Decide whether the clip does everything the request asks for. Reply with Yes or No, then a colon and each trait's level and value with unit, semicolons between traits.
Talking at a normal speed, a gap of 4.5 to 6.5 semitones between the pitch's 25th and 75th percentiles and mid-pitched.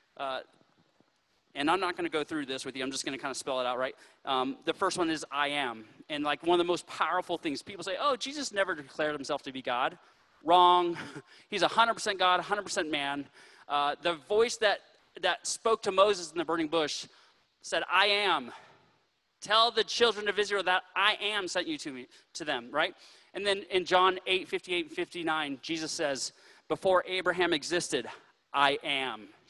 Yes: average, 195 wpm; wide, 5.6 semitones; medium, 180 Hz